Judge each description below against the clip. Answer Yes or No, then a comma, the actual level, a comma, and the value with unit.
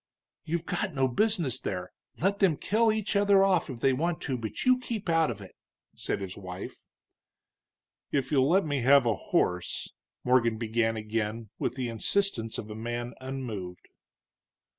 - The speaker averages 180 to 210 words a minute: No, average, 170 wpm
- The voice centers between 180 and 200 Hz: No, low, 130 Hz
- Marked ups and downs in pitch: Yes, wide, 7.6 semitones